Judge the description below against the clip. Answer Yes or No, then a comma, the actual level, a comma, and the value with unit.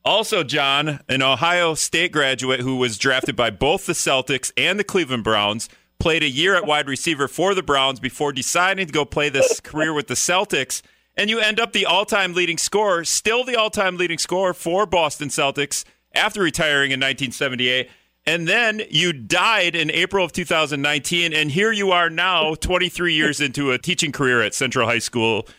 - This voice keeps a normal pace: Yes, average, 190 wpm